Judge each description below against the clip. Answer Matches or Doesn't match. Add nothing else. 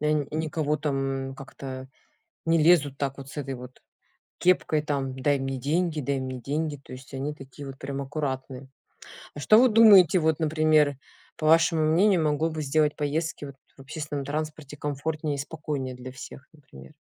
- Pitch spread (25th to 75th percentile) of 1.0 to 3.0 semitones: Matches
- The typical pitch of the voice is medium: Matches